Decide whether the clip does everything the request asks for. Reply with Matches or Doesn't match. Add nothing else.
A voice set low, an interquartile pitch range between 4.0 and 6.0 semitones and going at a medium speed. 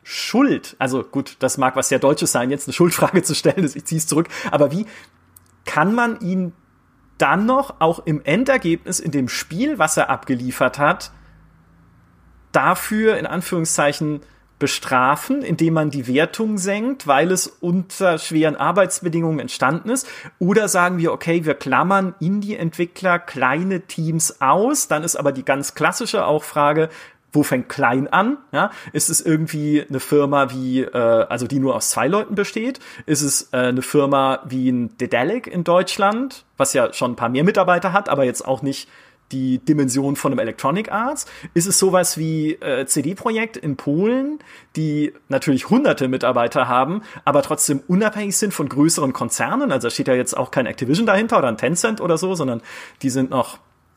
Doesn't match